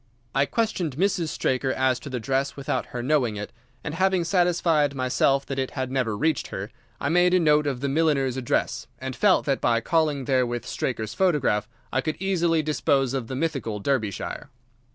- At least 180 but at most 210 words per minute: Yes, average, 190 wpm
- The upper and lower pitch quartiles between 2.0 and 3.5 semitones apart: No, average, 4.1 semitones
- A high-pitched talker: No, low, 135 Hz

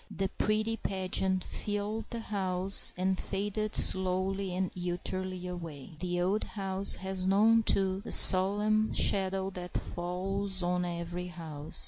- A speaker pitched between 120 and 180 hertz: No, high, 190 Hz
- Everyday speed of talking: No, slow, 130 wpm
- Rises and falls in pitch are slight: Yes, narrow, 1.8 semitones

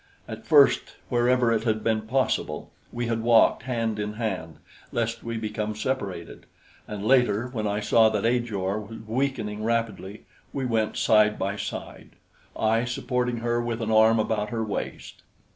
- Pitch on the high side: No, low, 110 Hz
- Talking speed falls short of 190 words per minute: Yes, average, 160 wpm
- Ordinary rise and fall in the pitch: No, narrow, 2.0 semitones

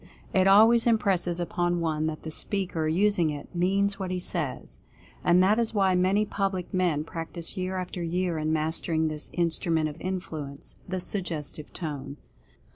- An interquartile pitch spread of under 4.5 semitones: Yes, average, 3.1 semitones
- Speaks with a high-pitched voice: No, medium, 175 Hz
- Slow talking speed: No, average, 170 wpm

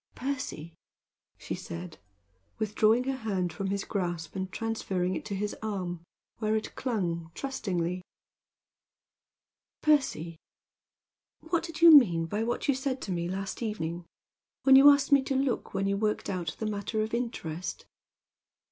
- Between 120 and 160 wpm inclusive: Yes, average, 145 wpm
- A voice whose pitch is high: Yes, high, 210 Hz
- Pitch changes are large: Yes, wide, 6.3 semitones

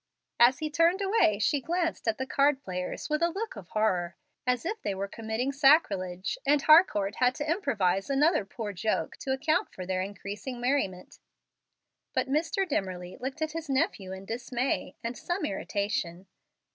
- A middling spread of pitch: No, wide, 7.5 semitones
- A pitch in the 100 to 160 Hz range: No, very high, 250 Hz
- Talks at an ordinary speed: Yes, average, 170 wpm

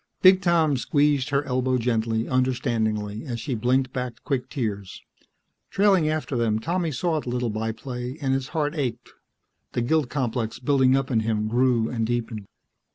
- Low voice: Yes, low, 125 Hz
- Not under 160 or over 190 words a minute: Yes, average, 165 wpm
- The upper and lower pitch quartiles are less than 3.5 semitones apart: No, average, 3.8 semitones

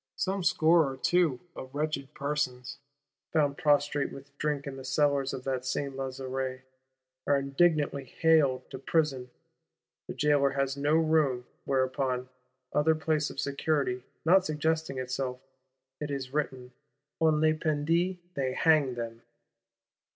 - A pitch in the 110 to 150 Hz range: Yes, medium, 140 Hz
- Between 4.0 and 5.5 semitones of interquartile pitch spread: No, average, 2.9 semitones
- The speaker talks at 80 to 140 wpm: Yes, slow, 135 wpm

